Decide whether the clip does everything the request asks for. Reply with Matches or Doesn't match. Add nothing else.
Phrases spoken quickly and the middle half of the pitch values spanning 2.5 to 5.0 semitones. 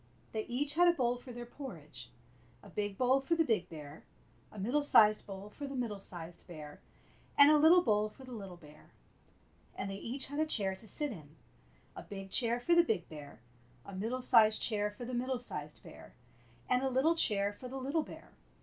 Doesn't match